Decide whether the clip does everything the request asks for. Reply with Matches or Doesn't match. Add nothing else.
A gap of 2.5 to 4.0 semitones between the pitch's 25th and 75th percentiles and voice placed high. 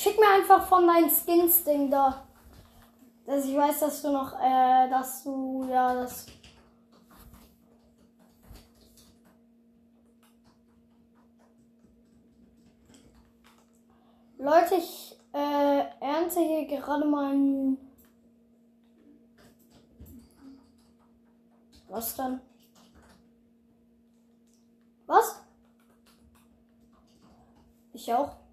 Matches